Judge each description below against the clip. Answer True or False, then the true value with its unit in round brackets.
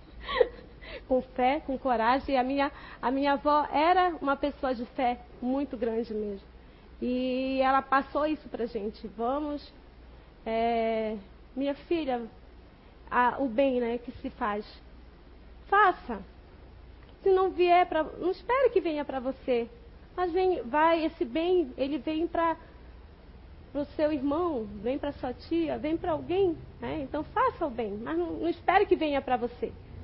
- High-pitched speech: True (280 Hz)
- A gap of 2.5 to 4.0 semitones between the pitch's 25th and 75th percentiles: False (4.9 semitones)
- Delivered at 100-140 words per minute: False (155 wpm)